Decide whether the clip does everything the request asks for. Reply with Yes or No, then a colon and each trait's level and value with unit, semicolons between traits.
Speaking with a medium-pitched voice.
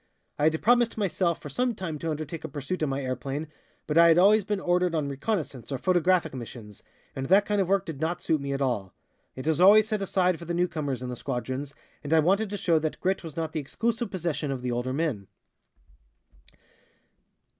Yes: medium, 160 Hz